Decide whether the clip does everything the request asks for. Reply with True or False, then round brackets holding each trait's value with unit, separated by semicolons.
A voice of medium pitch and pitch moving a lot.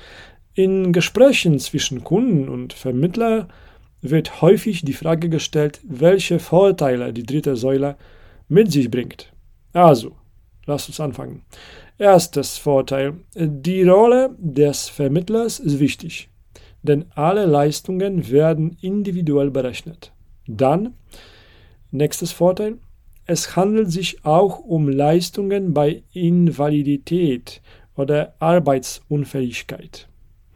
False (150 Hz; 5.0 semitones)